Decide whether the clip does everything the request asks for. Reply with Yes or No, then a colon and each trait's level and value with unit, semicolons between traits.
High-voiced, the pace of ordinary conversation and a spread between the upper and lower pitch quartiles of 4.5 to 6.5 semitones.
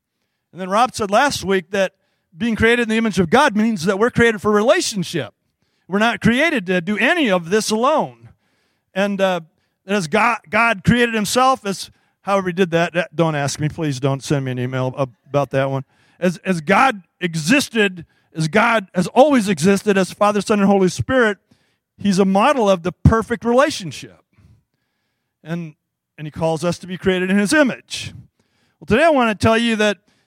Yes: high, 195 Hz; average, 185 wpm; average, 5.1 semitones